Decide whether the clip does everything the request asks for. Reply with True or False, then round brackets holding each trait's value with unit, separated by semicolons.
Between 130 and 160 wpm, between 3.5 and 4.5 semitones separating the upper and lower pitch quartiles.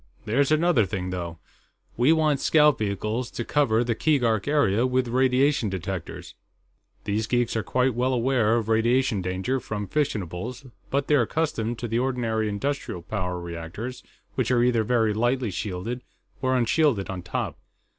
True (155 wpm; 4.0 semitones)